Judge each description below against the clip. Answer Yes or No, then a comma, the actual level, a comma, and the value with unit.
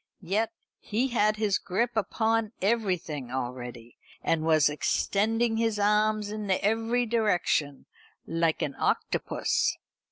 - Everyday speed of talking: No, slow, 115 wpm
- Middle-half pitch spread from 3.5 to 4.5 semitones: No, wide, 5.6 semitones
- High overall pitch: Yes, high, 210 Hz